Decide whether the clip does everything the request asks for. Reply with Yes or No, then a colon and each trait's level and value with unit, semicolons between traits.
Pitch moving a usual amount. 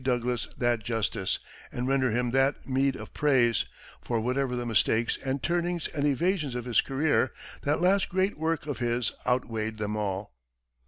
Yes: average, 3.6 semitones